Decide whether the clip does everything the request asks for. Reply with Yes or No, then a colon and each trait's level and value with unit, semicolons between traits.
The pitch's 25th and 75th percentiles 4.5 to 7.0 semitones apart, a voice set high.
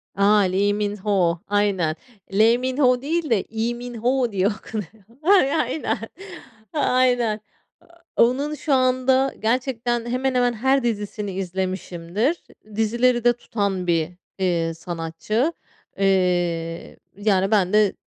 Yes: average, 4.8 semitones; high, 220 Hz